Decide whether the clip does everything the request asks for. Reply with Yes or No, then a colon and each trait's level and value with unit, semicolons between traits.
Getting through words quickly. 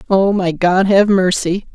No: average, 170 wpm